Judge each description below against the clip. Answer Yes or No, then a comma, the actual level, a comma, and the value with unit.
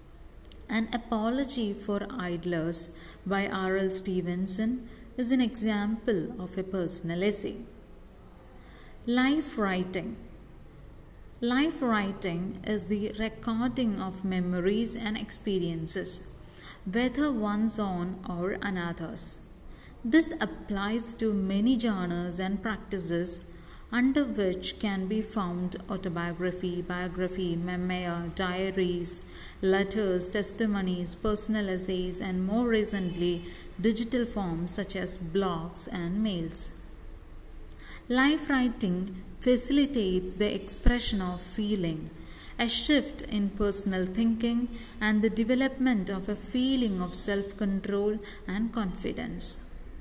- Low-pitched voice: No, high, 200 Hz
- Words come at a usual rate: No, slow, 100 wpm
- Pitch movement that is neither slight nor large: Yes, average, 3.8 semitones